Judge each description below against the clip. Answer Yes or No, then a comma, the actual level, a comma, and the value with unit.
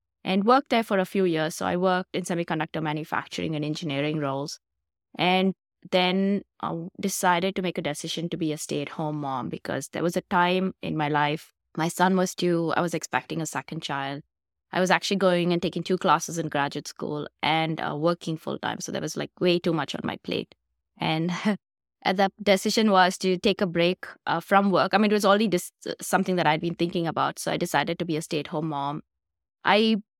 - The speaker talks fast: Yes, fast, 215 wpm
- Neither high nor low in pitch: Yes, medium, 175 Hz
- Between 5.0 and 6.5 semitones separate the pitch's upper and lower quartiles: No, average, 3.3 semitones